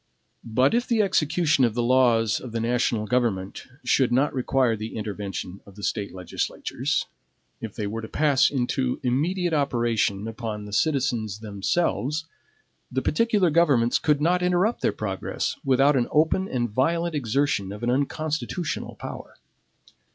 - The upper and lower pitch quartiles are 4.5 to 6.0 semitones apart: Yes, wide, 5.6 semitones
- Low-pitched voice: Yes, low, 125 Hz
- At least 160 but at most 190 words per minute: No, average, 150 wpm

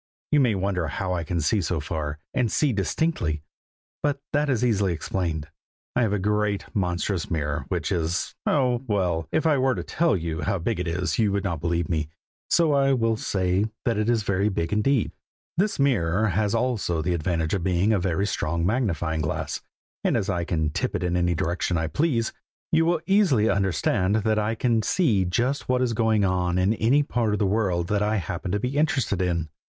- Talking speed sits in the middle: No, fast, 210 wpm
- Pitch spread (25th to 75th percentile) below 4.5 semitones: No, average, 5.2 semitones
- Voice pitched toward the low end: Yes, low, 100 Hz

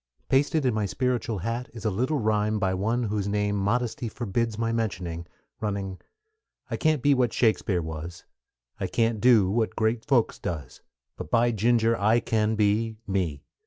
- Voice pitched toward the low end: Yes, low, 110 Hz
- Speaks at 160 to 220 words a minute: Yes, average, 165 wpm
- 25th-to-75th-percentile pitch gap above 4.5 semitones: No, average, 2.9 semitones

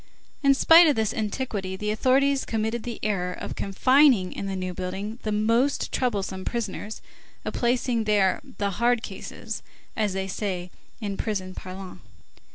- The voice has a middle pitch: No, high, 215 Hz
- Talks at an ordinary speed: Yes, average, 155 wpm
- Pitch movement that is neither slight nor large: Yes, average, 3.9 semitones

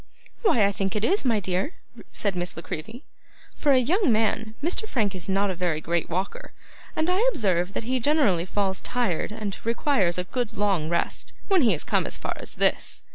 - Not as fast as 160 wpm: No, fast, 205 wpm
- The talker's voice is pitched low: No, high, 205 Hz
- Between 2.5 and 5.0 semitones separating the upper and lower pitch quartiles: No, wide, 5.5 semitones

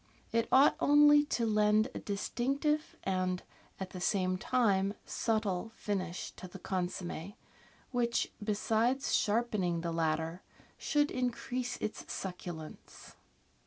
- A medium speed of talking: No, slow, 115 wpm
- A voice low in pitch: No, high, 210 Hz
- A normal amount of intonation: Yes, average, 4.9 semitones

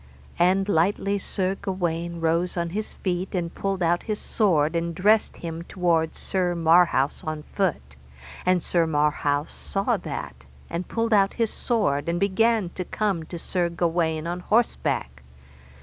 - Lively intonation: No, average, 3.1 semitones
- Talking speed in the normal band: Yes, average, 150 wpm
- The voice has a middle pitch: Yes, medium, 175 Hz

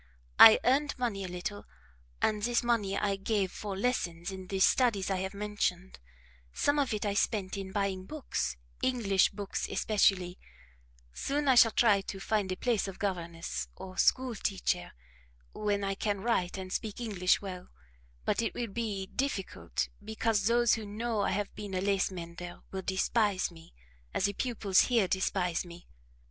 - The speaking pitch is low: No, high, 200 Hz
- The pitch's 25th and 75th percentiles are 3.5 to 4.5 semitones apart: No, average, 3.0 semitones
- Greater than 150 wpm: Yes, average, 170 wpm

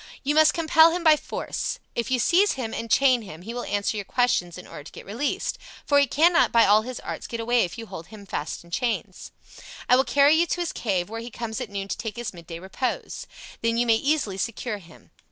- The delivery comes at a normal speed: No, fast, 240 wpm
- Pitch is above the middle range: Yes, high, 235 Hz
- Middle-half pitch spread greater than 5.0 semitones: Yes, wide, 5.5 semitones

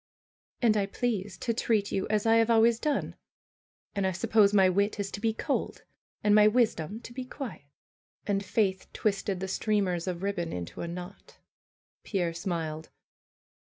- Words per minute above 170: No, average, 165 wpm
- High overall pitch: Yes, high, 200 Hz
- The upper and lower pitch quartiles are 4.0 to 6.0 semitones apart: No, average, 3.2 semitones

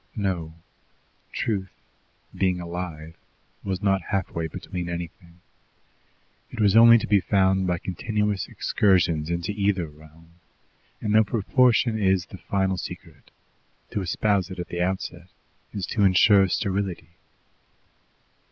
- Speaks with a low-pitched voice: Yes, very low, 95 Hz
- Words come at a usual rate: No, slow, 125 wpm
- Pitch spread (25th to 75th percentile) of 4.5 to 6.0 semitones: No, average, 2.8 semitones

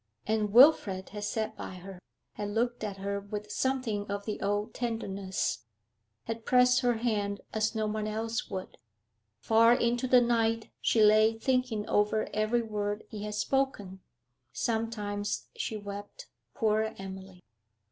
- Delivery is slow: No, average, 145 wpm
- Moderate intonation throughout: No, narrow, 2.0 semitones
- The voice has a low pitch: No, high, 215 Hz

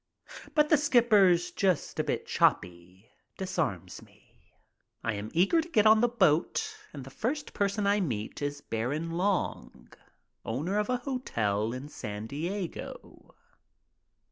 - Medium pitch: Yes, medium, 175 Hz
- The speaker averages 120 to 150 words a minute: Yes, average, 140 wpm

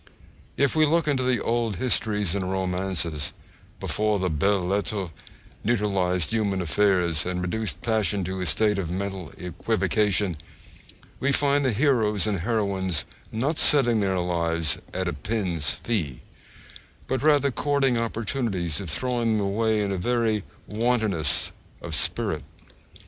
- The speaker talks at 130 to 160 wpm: Yes, slow, 135 wpm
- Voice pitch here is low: Yes, low, 100 Hz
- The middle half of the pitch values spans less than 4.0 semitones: No, average, 4.3 semitones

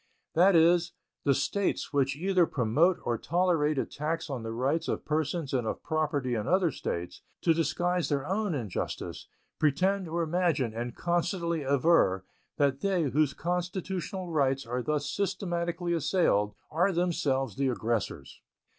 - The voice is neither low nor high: Yes, medium, 155 Hz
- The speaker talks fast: No, average, 145 wpm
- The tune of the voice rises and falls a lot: No, average, 4.7 semitones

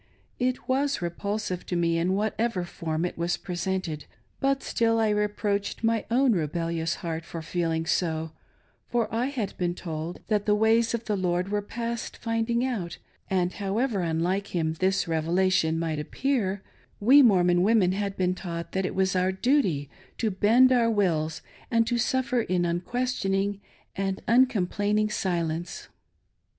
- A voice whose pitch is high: Yes, high, 195 Hz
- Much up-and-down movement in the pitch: No, average, 4.7 semitones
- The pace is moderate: Yes, average, 155 wpm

